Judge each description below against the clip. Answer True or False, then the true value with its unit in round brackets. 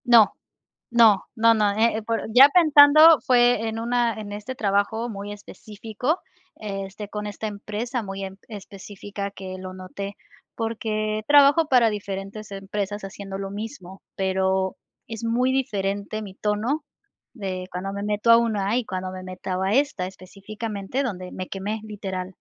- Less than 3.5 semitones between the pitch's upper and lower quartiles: True (2.9 semitones)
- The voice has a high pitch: True (210 Hz)